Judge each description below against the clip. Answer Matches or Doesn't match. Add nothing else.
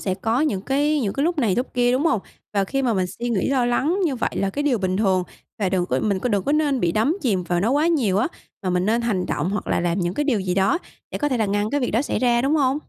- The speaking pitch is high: Matches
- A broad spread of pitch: Matches